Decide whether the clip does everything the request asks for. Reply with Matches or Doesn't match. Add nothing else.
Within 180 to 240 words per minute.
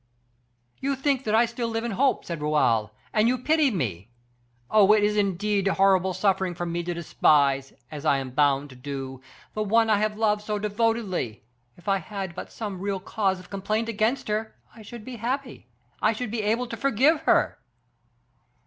Matches